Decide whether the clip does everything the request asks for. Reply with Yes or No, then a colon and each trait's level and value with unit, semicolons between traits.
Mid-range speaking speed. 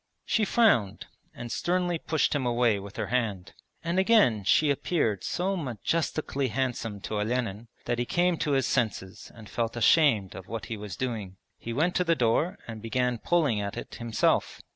Yes: average, 180 wpm